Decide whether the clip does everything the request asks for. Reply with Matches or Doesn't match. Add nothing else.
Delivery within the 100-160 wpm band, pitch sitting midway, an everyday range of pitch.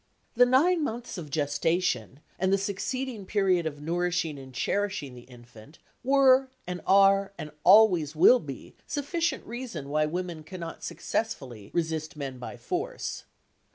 Doesn't match